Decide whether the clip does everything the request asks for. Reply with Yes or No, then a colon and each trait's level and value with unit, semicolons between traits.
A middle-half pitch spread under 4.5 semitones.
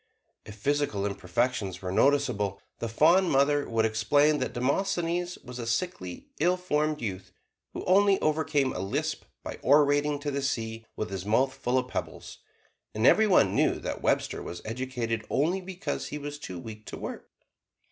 No: average, 5.3 semitones